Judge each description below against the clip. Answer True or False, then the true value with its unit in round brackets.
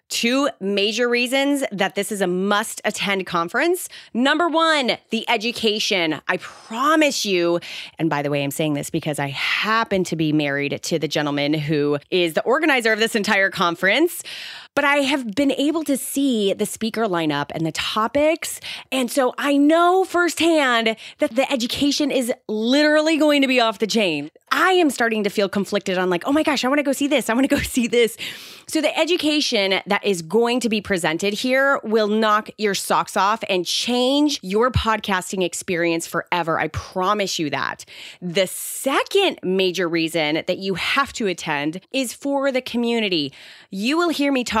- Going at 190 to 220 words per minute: False (180 wpm)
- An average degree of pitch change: False (7.1 semitones)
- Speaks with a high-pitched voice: True (220 Hz)